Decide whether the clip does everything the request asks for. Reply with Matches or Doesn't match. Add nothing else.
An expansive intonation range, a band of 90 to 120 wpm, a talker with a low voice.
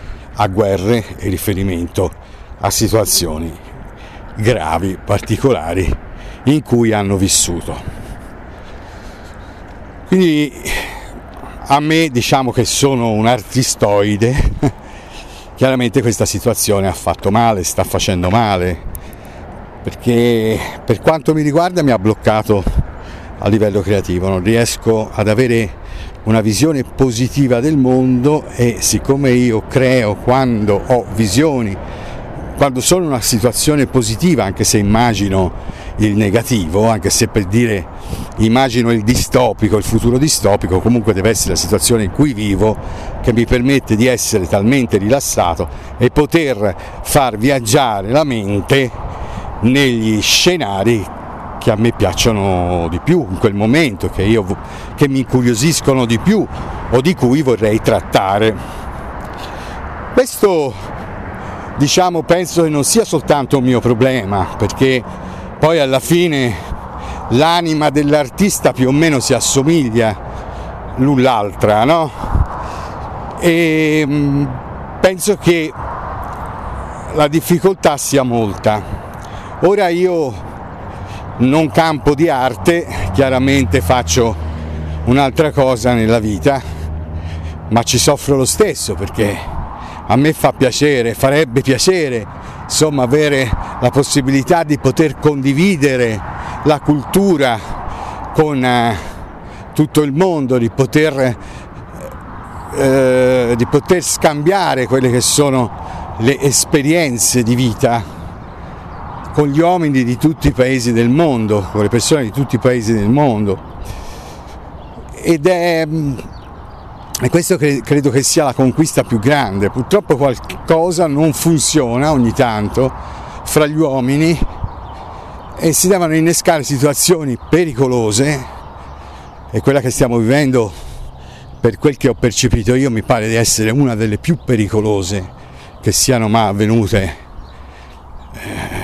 Matches